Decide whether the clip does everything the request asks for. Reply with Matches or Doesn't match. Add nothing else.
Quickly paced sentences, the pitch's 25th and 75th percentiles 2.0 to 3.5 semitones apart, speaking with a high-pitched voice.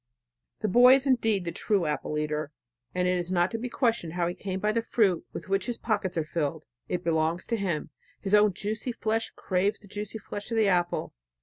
Doesn't match